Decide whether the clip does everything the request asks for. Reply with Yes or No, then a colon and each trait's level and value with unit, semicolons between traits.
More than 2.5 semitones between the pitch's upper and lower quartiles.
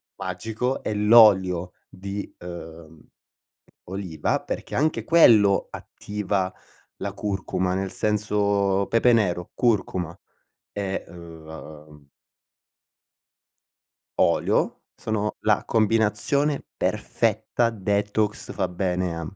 Yes: average, 2.9 semitones